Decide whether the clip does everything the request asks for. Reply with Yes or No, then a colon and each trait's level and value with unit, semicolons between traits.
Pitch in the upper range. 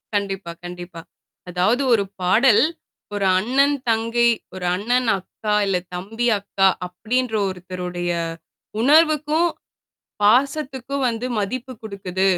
Yes: high, 220 Hz